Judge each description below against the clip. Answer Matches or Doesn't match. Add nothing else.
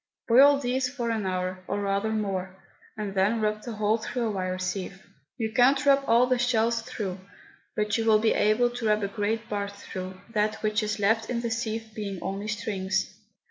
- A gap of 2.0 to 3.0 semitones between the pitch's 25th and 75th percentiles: Matches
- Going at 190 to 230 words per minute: Matches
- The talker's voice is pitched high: Matches